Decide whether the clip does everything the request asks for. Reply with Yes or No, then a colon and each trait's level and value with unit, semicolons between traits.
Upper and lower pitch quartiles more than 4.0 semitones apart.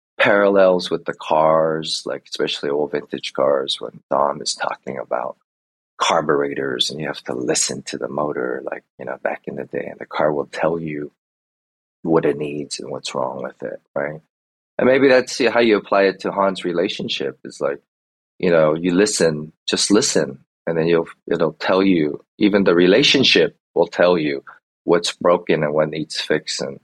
Yes: average, 4.9 semitones